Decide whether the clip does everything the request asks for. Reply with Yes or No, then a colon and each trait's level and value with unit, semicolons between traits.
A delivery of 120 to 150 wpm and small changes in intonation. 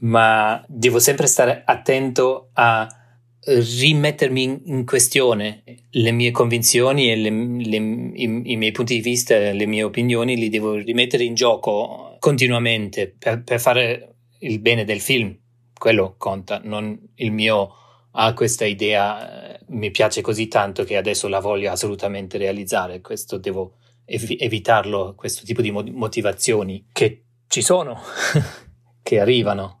Yes: average, 140 wpm; narrow, 2.3 semitones